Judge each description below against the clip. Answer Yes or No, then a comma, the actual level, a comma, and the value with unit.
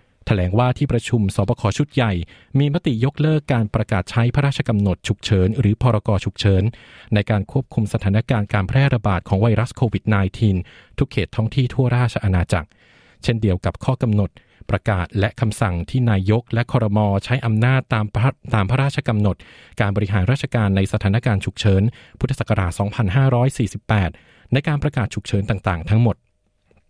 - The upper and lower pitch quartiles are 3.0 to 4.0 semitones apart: Yes, average, 3.7 semitones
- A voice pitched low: Yes, low, 110 Hz